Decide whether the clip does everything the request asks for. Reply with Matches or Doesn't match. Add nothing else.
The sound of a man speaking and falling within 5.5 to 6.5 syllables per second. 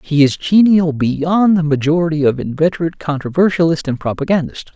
Matches